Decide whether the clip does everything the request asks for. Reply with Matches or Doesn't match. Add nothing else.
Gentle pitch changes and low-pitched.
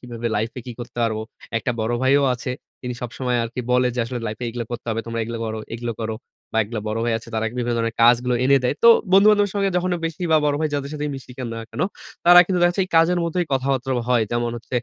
Doesn't match